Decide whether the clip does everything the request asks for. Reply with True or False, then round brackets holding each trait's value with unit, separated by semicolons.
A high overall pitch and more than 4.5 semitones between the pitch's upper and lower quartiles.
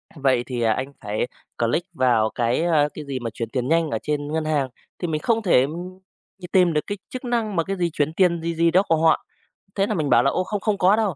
False (160 Hz; 5.6 semitones)